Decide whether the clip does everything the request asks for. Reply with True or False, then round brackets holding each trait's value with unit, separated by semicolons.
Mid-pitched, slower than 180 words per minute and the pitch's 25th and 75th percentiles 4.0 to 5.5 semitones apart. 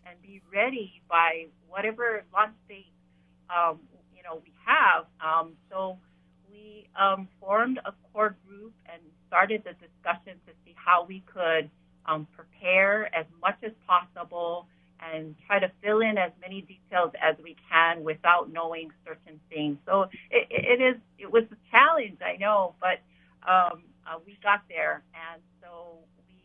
False (180 Hz; 155 wpm; 3.3 semitones)